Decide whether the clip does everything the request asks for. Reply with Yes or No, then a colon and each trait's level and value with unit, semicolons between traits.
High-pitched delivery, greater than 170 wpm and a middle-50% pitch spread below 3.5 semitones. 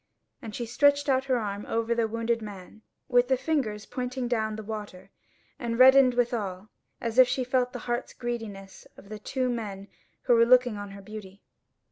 Yes: high, 230 Hz; average, 185 wpm; average, 3.0 semitones